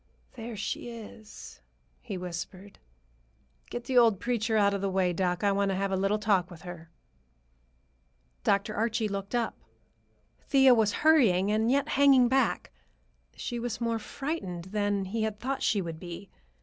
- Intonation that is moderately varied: Yes, average, 3.7 semitones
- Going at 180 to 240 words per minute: No, average, 160 wpm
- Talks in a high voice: Yes, high, 210 Hz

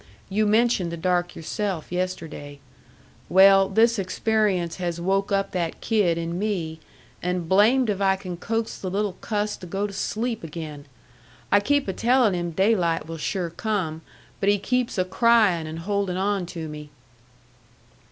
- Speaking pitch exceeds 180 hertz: Yes, high, 190 Hz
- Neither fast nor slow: Yes, average, 160 wpm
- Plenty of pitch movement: No, average, 3.6 semitones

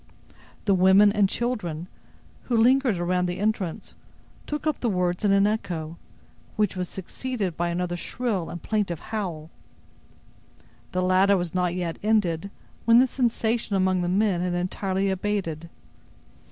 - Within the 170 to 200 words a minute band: No, average, 145 wpm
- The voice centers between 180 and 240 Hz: Yes, high, 190 Hz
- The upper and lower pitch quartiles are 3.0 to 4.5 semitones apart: Yes, average, 3.4 semitones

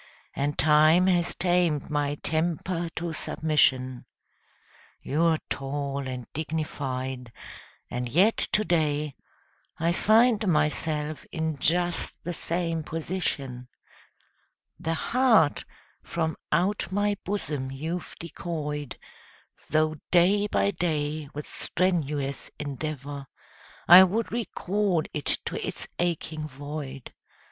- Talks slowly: Yes, slow, 105 wpm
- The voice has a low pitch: No, medium, 155 Hz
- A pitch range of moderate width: Yes, average, 3.3 semitones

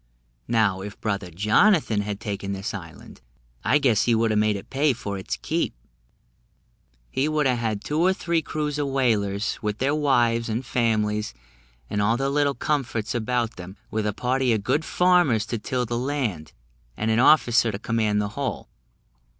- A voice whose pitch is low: Yes, low, 115 Hz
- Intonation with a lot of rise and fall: No, average, 4.6 semitones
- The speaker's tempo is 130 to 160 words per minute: No, average, 180 wpm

